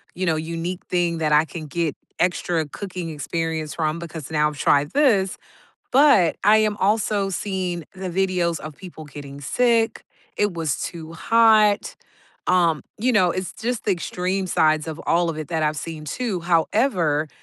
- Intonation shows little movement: No, average, 3.7 semitones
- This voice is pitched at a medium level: Yes, medium, 170 Hz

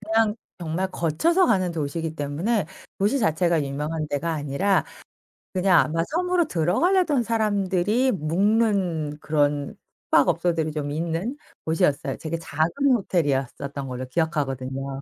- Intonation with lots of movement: Yes, wide, 5.8 semitones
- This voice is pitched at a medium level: Yes, medium, 165 Hz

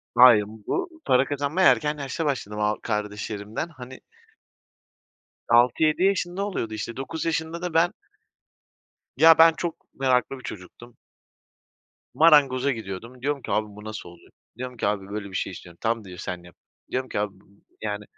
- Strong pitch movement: Yes, wide, 6.6 semitones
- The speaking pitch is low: Yes, low, 125 Hz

